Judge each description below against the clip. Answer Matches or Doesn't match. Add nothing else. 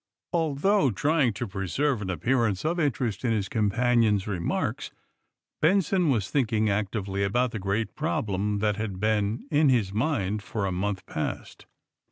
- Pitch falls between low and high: Doesn't match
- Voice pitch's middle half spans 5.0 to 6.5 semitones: Matches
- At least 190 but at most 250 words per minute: Doesn't match